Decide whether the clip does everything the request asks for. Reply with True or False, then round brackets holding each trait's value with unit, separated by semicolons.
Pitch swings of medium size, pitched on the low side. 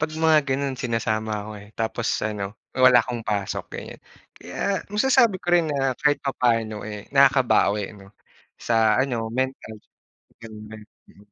True (4.2 semitones; 120 Hz)